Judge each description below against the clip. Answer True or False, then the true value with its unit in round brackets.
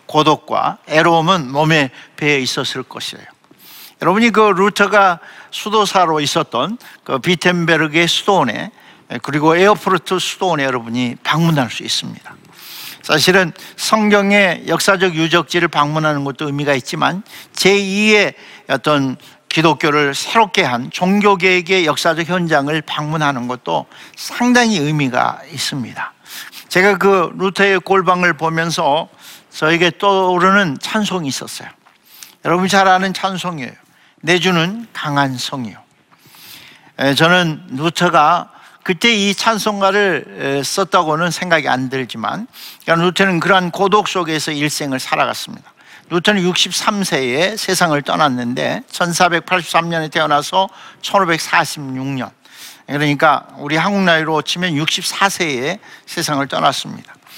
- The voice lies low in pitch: False (170 Hz)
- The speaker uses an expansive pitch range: False (4.3 semitones)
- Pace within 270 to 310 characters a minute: True (280 characters per minute)